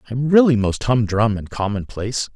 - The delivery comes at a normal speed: Yes, average, 155 wpm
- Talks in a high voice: No, low, 115 Hz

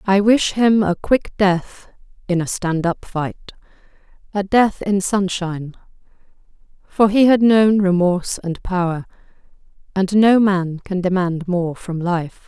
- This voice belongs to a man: No, female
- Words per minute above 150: No, average, 140 wpm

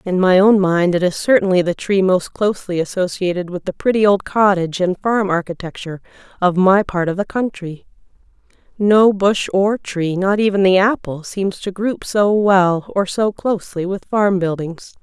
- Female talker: Yes, female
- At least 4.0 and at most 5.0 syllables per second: Yes, 4.8 syllables/s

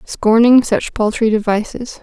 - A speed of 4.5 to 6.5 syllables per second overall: No, 4.2 syllables/s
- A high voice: Yes, high, 225 Hz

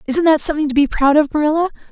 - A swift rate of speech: Yes, fast, 250 wpm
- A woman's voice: Yes, female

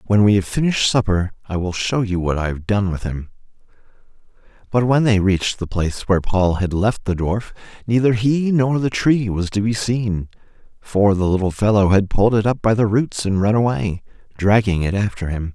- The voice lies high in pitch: No, low, 105 Hz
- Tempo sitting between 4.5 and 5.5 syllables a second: Yes, 5.3 syllables/s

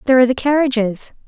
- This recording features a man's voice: No, female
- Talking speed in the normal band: Yes, average, 190 wpm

